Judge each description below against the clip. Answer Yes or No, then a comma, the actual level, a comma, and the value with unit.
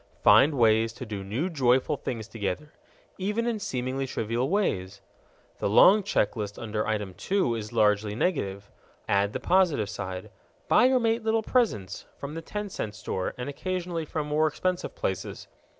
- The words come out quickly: No, average, 165 wpm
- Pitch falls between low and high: No, low, 125 Hz